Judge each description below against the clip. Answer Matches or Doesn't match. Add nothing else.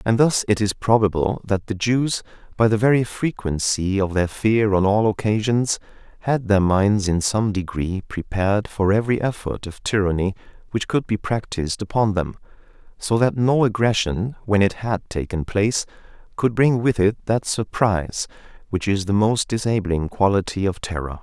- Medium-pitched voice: Doesn't match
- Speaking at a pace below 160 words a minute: Doesn't match